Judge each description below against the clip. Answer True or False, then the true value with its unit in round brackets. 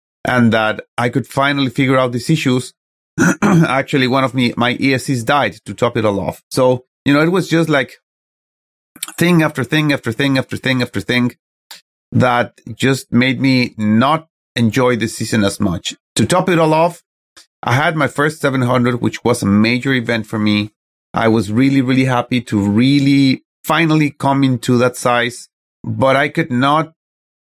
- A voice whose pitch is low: True (130 Hz)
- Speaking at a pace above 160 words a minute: True (175 wpm)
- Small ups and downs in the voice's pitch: False (3.2 semitones)